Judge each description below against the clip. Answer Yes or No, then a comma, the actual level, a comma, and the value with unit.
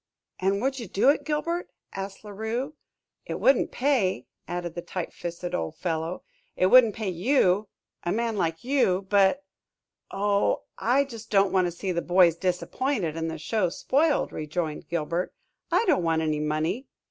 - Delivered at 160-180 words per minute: Yes, average, 170 wpm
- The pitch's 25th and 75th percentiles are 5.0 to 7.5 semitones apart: Yes, wide, 5.5 semitones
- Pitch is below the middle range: No, high, 190 Hz